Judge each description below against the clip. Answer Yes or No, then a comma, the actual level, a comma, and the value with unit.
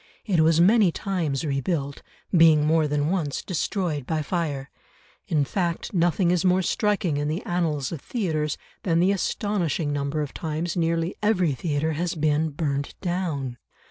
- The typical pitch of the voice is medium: Yes, medium, 165 Hz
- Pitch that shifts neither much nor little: Yes, average, 3.3 semitones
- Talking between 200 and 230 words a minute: No, average, 155 wpm